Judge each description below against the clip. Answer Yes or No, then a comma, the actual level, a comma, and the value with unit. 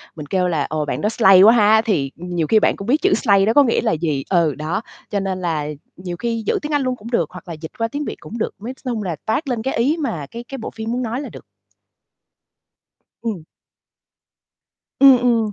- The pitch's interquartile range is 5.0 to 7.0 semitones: Yes, wide, 5.4 semitones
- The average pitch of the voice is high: Yes, high, 215 Hz